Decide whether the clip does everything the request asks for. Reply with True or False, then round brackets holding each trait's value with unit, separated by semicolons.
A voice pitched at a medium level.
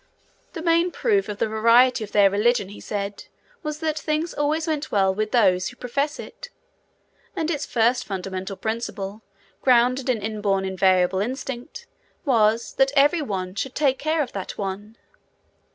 False (235 Hz)